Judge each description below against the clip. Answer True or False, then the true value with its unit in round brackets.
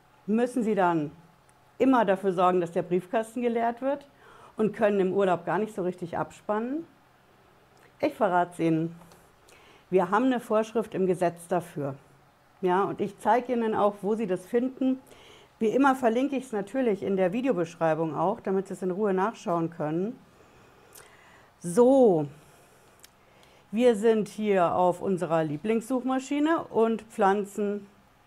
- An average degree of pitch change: True (4.7 semitones)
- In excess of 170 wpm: False (140 wpm)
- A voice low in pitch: False (195 Hz)